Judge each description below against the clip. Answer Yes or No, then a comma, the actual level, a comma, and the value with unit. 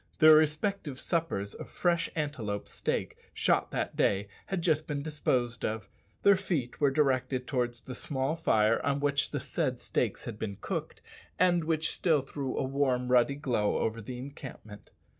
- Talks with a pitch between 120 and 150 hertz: Yes, medium, 140 Hz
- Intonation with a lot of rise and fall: No, average, 4.4 semitones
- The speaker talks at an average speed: Yes, average, 165 wpm